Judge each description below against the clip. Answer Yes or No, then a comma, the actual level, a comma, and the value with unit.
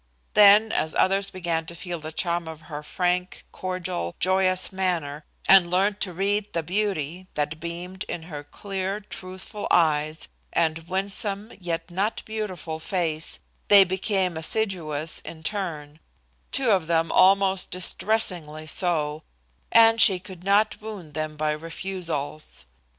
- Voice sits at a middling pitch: Yes, medium, 180 Hz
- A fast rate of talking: No, slow, 135 wpm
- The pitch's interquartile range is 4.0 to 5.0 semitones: No, average, 3.4 semitones